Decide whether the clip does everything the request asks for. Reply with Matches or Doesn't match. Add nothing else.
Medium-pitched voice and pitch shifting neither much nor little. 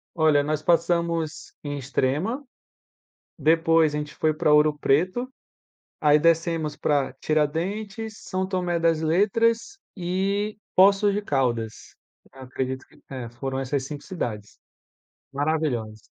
Matches